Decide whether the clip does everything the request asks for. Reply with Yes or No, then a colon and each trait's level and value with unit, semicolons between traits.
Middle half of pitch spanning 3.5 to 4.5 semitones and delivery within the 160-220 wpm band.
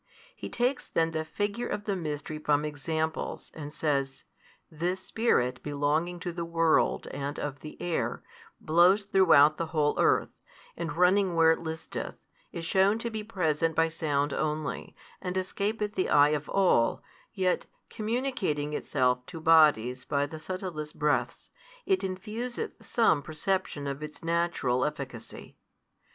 No: average, 4.2 semitones; average, 145 wpm